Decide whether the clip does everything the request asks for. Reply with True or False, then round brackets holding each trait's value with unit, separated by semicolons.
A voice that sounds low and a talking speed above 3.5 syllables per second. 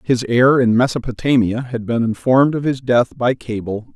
True (125 Hz; 5.0 syllables/s)